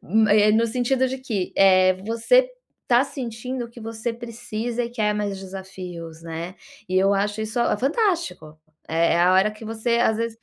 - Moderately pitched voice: No, high, 220 Hz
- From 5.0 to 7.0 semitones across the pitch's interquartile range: No, average, 3.9 semitones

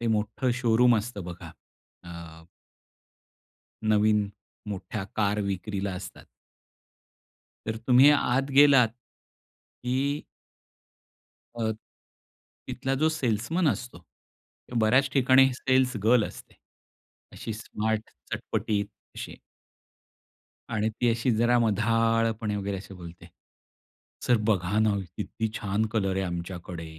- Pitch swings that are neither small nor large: Yes, average, 3.6 semitones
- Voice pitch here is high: No, low, 110 Hz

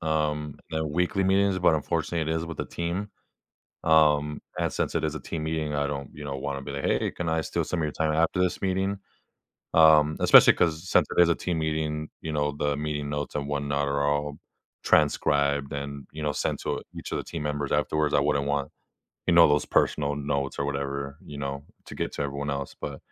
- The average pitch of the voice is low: Yes, very low, 75 Hz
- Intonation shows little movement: Yes, narrow, 2.0 semitones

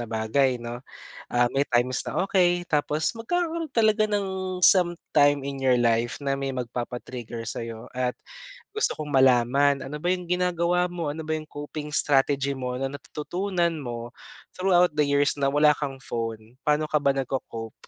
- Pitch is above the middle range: No, medium, 145 Hz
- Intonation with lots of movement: Yes, wide, 5.7 semitones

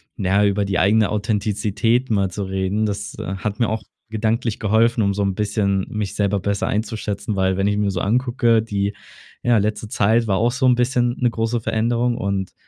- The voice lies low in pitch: Yes, low, 105 Hz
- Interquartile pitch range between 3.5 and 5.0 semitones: No, narrow, 2.4 semitones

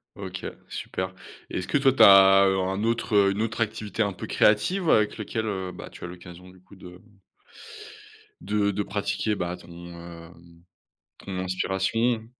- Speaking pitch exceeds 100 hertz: No, very low, 95 Hz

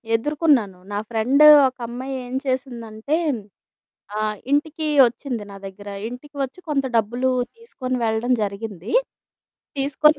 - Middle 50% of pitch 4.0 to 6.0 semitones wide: Yes, average, 4.4 semitones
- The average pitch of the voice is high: Yes, very high, 250 Hz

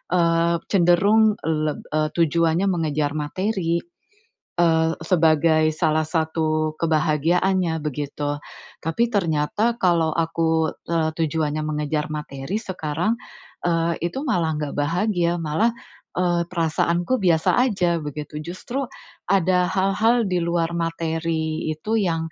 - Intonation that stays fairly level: Yes, narrow, 2.3 semitones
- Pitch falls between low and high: Yes, medium, 165 Hz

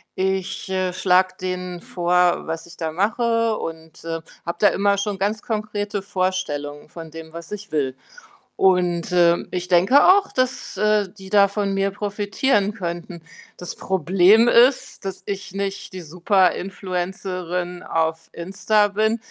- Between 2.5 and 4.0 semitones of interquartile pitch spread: Yes, average, 2.8 semitones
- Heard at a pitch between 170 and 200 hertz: Yes, high, 190 Hz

